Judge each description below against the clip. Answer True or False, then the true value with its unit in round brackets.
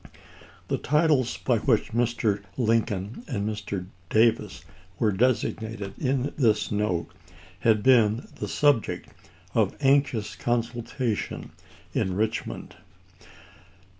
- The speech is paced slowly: True (100 wpm)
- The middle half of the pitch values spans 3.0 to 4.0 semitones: True (3.3 semitones)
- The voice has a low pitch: True (115 Hz)